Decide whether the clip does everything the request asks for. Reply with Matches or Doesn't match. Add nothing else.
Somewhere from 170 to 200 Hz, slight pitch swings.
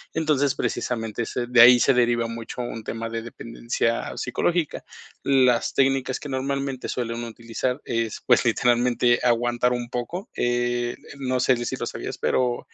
Doesn't match